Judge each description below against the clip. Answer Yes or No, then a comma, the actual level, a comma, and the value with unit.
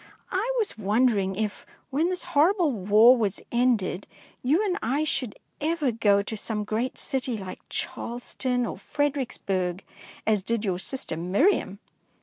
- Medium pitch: No, high, 235 Hz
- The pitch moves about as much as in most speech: No, wide, 5.9 semitones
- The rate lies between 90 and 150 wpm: Yes, average, 140 wpm